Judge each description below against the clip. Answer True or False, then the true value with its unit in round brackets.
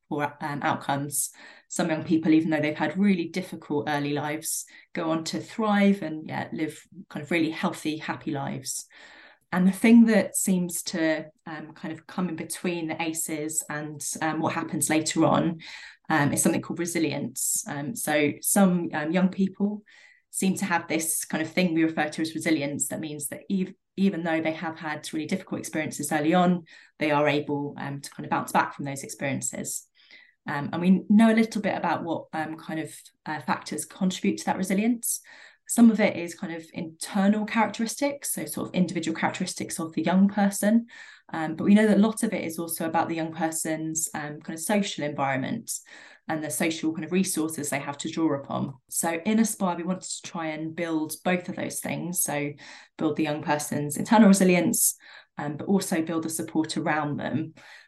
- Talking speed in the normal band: True (195 wpm)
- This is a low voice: False (165 Hz)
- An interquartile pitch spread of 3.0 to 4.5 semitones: True (3.5 semitones)